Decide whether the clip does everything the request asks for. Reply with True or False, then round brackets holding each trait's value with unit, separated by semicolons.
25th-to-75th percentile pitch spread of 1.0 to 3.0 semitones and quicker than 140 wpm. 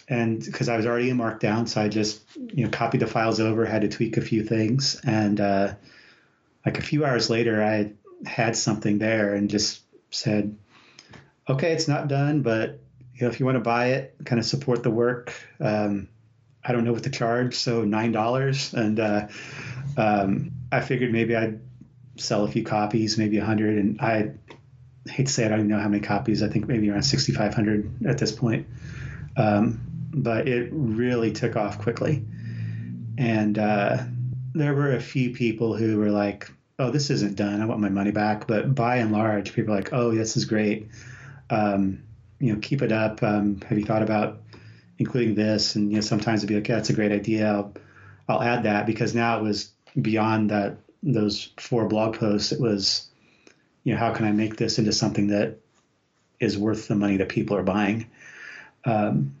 True (2.6 semitones; 200 wpm)